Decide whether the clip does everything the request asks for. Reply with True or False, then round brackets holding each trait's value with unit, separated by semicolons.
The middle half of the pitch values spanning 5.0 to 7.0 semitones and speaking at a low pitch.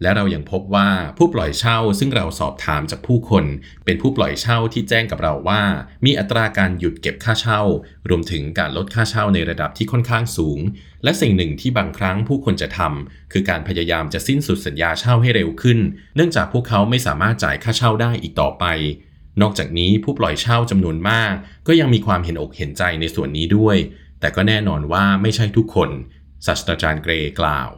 True (5.6 semitones; 100 Hz)